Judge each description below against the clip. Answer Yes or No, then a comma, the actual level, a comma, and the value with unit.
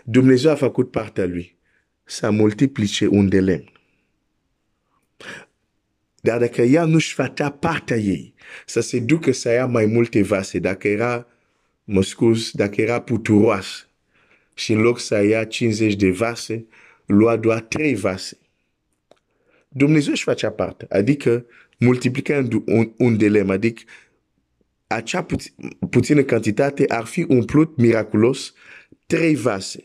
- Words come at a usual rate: No, slow, 85 wpm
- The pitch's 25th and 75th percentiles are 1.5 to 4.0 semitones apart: Yes, average, 3.4 semitones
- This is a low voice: Yes, low, 115 Hz